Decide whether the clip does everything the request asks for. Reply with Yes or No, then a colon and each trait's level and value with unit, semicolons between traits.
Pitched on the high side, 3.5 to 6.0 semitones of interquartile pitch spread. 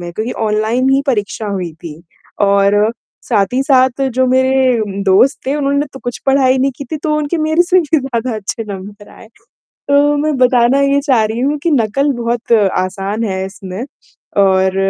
Yes: high, 245 Hz; average, 5.1 semitones